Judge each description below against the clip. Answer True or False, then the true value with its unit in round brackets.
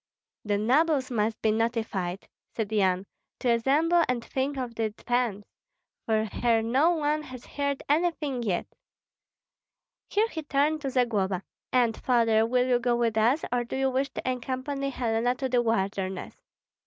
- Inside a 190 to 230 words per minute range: False (155 wpm)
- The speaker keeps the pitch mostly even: False (3.6 semitones)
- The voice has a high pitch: True (245 Hz)